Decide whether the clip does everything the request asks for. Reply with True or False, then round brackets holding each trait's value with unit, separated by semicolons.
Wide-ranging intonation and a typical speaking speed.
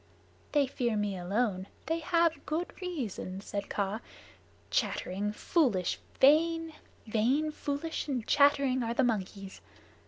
False (7.0 semitones; 120 wpm)